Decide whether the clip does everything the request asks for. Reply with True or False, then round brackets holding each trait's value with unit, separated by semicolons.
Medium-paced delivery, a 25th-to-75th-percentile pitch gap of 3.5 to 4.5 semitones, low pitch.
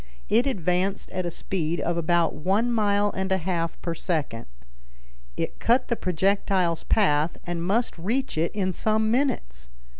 False (155 wpm; 4.0 semitones; 185 Hz)